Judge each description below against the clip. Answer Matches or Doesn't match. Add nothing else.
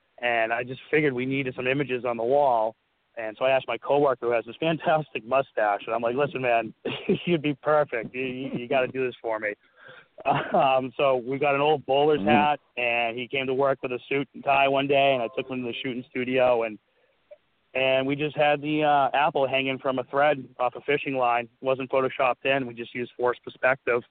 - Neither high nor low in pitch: Doesn't match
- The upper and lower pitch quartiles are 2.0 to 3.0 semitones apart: Matches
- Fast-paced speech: Matches